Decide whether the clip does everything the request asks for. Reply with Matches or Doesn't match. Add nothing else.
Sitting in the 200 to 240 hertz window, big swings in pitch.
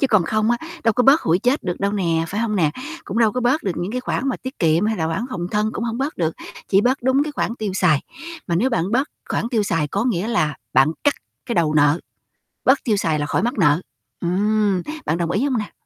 Matches